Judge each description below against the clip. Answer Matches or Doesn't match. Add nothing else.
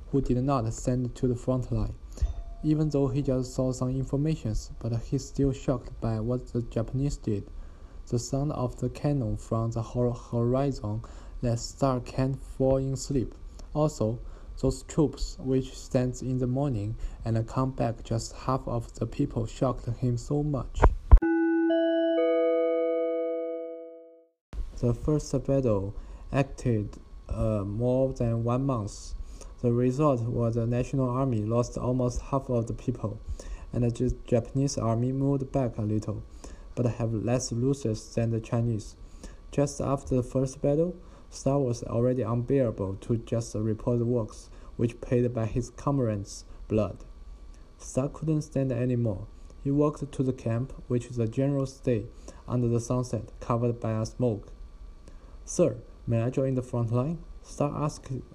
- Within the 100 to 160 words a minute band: Matches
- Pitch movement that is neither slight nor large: Matches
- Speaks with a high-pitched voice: Doesn't match